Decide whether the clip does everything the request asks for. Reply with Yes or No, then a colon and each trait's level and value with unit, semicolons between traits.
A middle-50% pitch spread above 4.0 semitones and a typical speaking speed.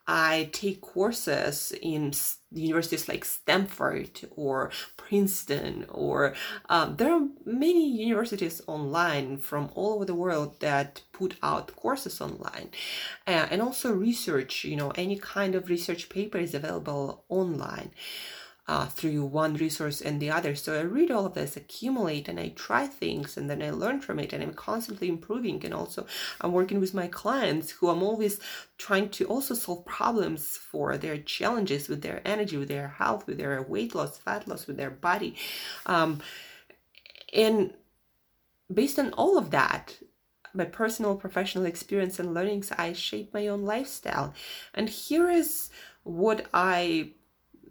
Yes: wide, 5.4 semitones; average, 155 wpm